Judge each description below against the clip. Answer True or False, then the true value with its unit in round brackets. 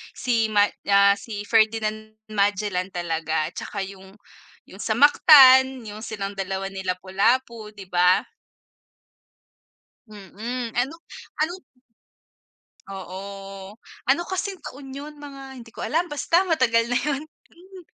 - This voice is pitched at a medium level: False (215 Hz)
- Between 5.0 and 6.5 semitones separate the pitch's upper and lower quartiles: True (5.3 semitones)